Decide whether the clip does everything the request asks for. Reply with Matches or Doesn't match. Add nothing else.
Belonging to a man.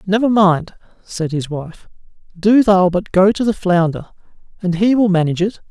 Matches